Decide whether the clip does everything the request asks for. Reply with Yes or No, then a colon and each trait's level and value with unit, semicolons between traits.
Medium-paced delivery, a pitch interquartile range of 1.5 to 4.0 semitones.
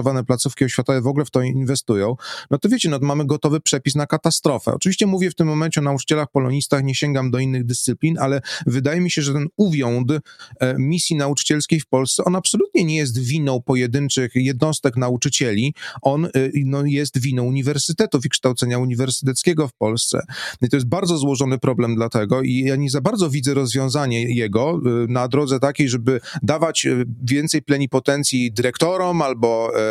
No: fast, 175 wpm; average, 2.9 semitones